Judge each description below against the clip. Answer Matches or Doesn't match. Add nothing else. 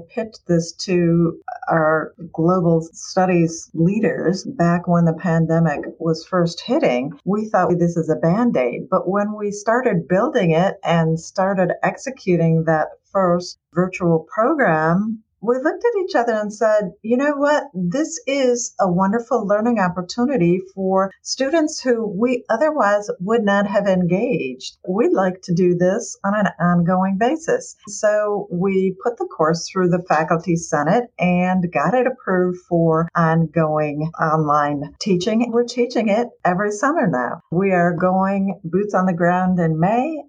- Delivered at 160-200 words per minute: Doesn't match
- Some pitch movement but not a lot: Matches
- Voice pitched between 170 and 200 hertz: Matches